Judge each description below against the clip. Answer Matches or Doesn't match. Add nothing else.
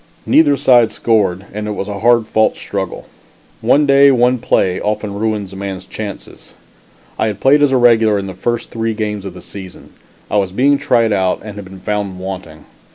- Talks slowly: Doesn't match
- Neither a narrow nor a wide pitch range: Matches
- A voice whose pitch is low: Matches